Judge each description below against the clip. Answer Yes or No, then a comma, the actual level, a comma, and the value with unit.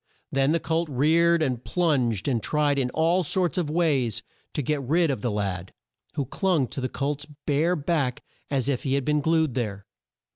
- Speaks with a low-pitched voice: No, medium, 145 Hz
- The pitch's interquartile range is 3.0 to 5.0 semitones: Yes, average, 4.2 semitones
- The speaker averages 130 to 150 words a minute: No, average, 190 wpm